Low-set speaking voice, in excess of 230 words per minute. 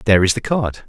Yes: low, 110 Hz; fast, 275 wpm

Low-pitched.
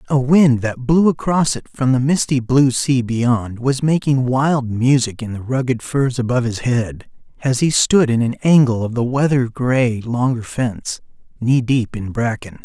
Yes: low, 125 Hz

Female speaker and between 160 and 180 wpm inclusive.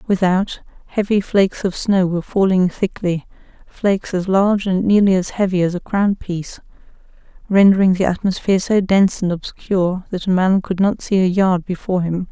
Yes: female; average, 175 wpm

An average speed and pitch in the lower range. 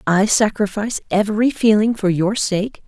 No: average, 145 wpm; high, 205 Hz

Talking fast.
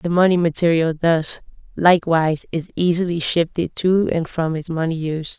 No: average, 155 wpm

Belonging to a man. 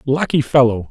Yes: male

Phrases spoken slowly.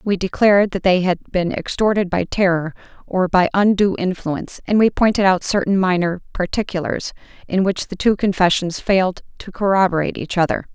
No: average, 170 wpm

